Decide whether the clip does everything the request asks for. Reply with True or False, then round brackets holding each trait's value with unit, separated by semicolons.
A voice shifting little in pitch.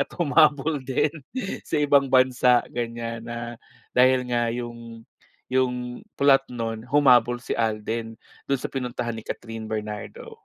True (2.2 semitones)